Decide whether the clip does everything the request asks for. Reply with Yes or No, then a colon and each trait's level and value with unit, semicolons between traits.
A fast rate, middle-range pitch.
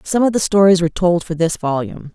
Yes: fast, 250 wpm; medium, 175 Hz